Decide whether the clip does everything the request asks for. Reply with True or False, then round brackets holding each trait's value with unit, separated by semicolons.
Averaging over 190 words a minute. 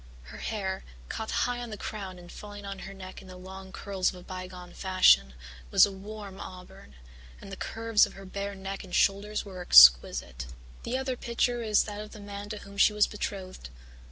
True (205 wpm)